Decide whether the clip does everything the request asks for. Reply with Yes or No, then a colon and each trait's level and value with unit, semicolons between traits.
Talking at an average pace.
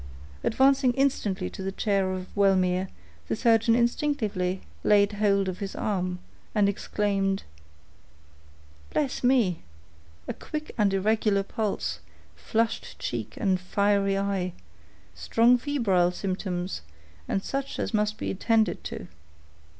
No: slow, 110 wpm